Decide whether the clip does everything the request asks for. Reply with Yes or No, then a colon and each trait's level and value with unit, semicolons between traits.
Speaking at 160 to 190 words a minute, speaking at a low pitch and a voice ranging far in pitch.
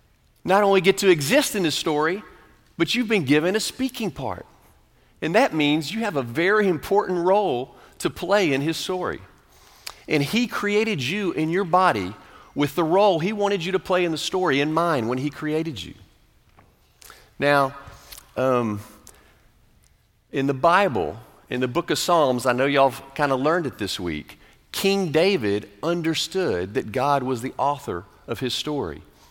No: average, 170 wpm; medium, 160 Hz; wide, 5.8 semitones